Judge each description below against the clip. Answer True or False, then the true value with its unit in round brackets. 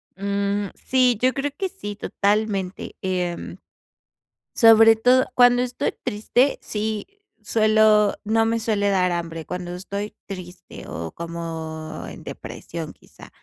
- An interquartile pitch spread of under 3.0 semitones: False (3.9 semitones)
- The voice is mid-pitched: False (205 Hz)